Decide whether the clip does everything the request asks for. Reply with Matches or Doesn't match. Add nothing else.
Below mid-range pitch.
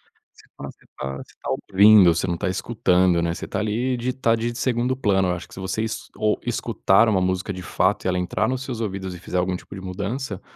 Matches